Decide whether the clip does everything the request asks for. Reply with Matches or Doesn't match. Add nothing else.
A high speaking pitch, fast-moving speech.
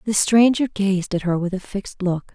Matches